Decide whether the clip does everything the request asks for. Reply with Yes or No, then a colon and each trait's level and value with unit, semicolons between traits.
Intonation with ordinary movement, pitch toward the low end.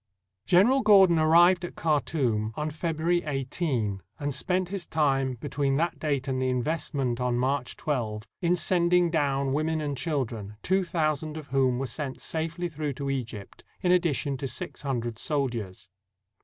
No: average, 4.4 semitones; medium, 145 Hz